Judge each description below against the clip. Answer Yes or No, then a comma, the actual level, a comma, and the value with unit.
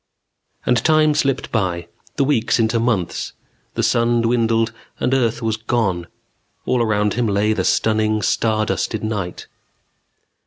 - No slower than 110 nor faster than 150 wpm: Yes, average, 140 wpm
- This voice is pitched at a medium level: No, low, 115 Hz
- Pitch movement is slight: Yes, narrow, 2.0 semitones